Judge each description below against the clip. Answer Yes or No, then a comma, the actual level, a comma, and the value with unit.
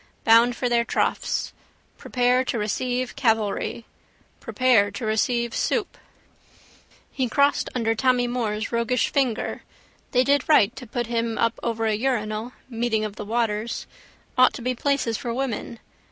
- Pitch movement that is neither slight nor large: No, narrow, 2.2 semitones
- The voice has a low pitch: No, high, 235 Hz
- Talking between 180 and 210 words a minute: No, average, 145 wpm